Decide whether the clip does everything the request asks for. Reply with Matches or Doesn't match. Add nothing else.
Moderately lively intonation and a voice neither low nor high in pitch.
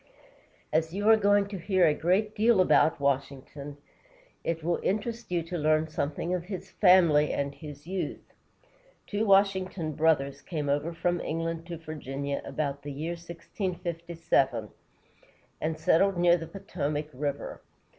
Matches